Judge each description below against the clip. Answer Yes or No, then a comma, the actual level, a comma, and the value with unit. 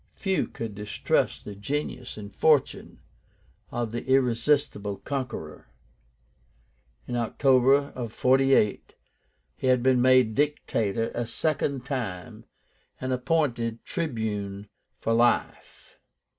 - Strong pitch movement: No, average, 3.6 semitones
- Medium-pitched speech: No, low, 125 Hz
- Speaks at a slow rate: Yes, slow, 105 wpm